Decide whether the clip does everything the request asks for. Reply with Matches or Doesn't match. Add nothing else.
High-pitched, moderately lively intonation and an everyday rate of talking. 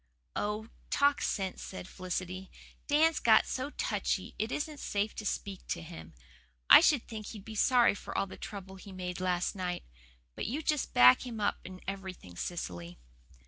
Matches